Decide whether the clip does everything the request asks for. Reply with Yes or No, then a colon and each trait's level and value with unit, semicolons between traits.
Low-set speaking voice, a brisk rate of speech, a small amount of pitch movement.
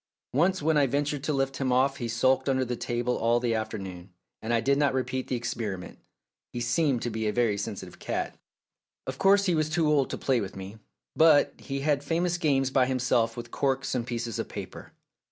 No: low, 130 Hz; fast, 215 wpm; average, 3.5 semitones